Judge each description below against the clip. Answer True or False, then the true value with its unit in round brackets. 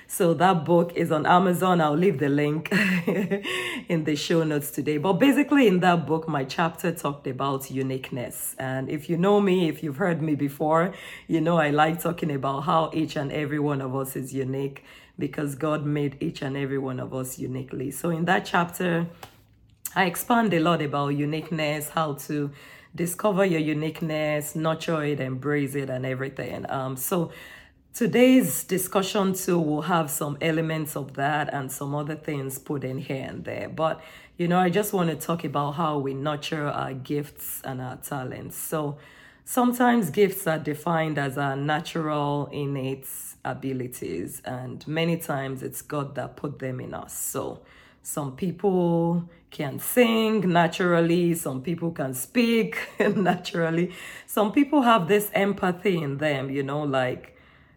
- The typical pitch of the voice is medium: True (155 Hz)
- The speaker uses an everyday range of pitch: True (3.9 semitones)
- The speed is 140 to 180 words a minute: True (165 wpm)